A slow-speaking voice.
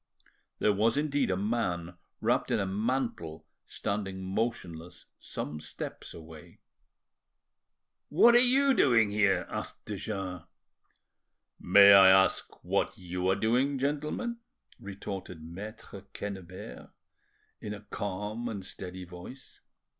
Yes: slow, 115 wpm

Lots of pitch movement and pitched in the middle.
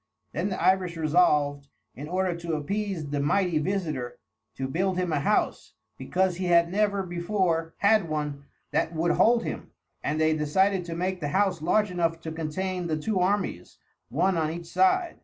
No: average, 3.4 semitones; medium, 175 Hz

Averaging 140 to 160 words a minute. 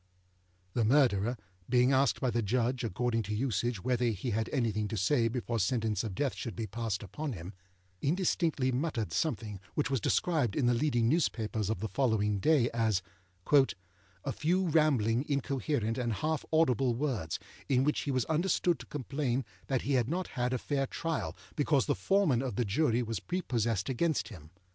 No: average, 175 wpm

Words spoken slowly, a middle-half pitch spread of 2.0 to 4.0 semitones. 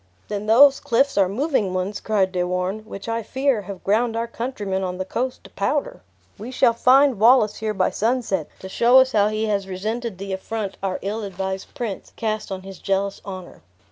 No: average, 200 wpm; average, 3.5 semitones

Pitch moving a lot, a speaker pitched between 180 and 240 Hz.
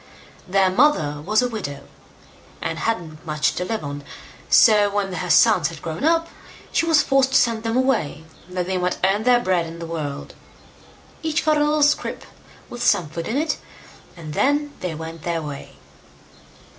Yes: wide, 7.9 semitones; high, 190 Hz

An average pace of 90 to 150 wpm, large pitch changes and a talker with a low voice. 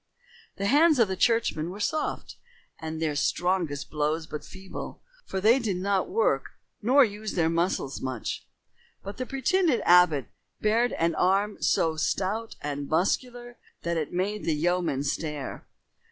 No: average, 145 wpm; wide, 6.1 semitones; medium, 185 Hz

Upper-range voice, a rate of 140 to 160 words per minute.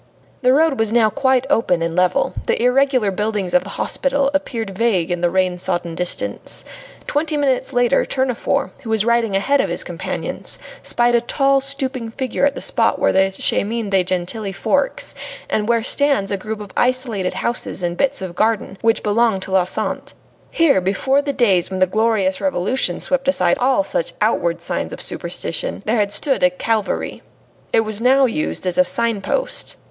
No: high, 225 Hz; average, 185 wpm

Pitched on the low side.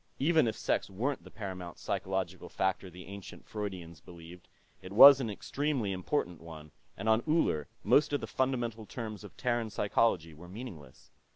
Yes: low, 100 Hz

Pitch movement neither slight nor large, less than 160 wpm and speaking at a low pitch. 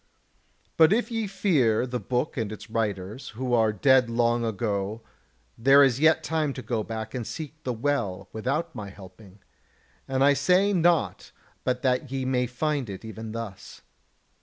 No: average, 4.5 semitones; average, 165 wpm; low, 125 Hz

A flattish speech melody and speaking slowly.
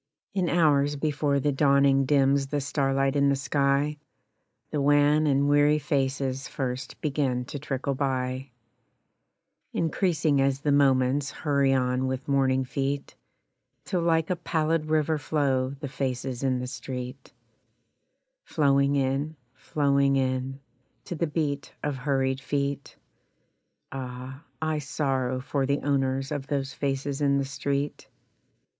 Yes: narrow, 1.6 semitones; slow, 130 wpm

